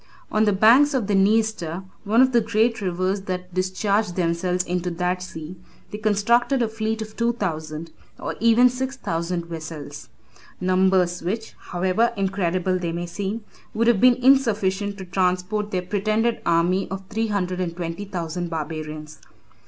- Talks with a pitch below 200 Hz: Yes, high, 190 Hz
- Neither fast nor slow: Yes, average, 165 wpm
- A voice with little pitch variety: No, average, 3.7 semitones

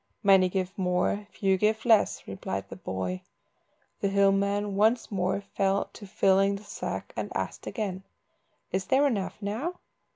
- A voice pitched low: No, high, 195 Hz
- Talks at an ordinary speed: Yes, average, 155 wpm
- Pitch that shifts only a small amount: Yes, narrow, 1.7 semitones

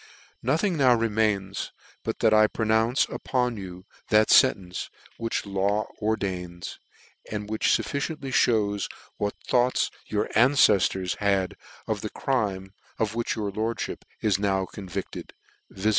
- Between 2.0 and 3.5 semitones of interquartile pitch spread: Yes, average, 3.0 semitones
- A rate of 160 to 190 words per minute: No, slow, 135 wpm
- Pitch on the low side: Yes, low, 105 Hz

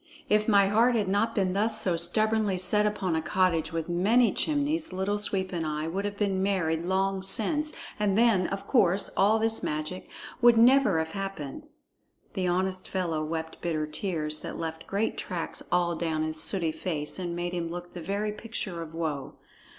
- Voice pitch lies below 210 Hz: Yes, high, 190 Hz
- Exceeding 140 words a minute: Yes, average, 185 wpm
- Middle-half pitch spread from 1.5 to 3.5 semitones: No, average, 4.0 semitones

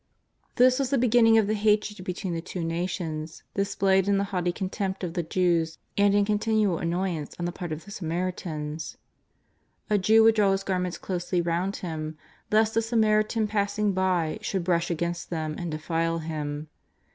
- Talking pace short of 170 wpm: No, average, 180 wpm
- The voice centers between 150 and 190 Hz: Yes, medium, 185 Hz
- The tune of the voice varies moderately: Yes, average, 3.7 semitones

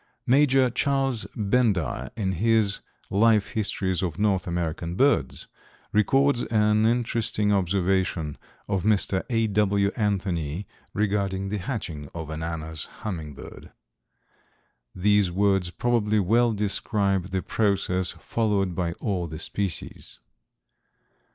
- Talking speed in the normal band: No, slow, 110 wpm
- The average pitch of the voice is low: Yes, low, 100 Hz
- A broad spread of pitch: No, average, 3.3 semitones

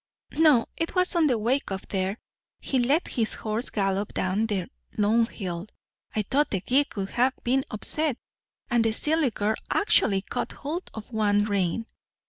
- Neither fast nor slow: Yes, average, 170 wpm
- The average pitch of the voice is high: Yes, high, 225 Hz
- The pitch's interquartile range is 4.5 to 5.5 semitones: Yes, average, 5.0 semitones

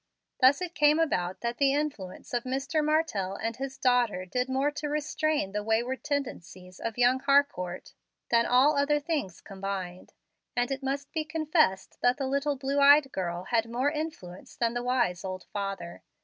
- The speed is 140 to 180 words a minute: Yes, average, 175 wpm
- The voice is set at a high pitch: Yes, very high, 255 Hz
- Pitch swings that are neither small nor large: No, wide, 6.4 semitones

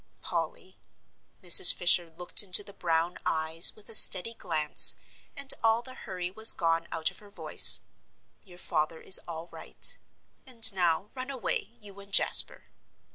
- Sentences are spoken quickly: No, average, 155 wpm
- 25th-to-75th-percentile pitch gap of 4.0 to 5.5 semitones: Yes, average, 5.0 semitones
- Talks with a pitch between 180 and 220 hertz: Yes, medium, 185 Hz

